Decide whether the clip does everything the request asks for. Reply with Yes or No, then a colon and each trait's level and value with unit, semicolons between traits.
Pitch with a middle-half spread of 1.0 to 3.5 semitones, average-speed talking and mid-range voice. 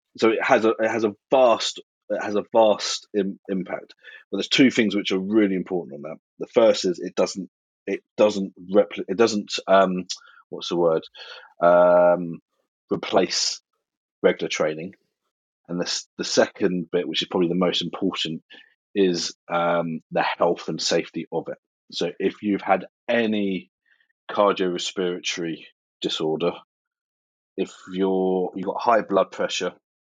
No: average, 2.7 semitones; average, 150 wpm; very low, 95 Hz